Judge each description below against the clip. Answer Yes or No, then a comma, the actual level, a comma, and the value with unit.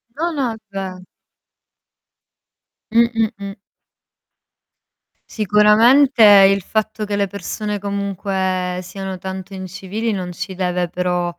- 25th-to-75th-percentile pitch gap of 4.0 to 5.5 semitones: No, narrow, 2.6 semitones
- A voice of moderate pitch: No, high, 200 Hz